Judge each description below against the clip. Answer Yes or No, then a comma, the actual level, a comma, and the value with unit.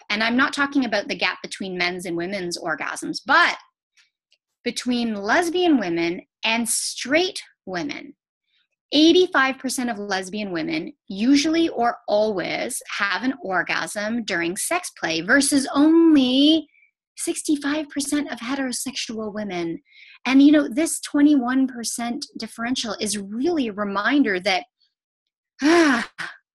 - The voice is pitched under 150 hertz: No, very high, 265 Hz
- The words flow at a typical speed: No, slow, 115 wpm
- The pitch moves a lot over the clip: Yes, wide, 6.1 semitones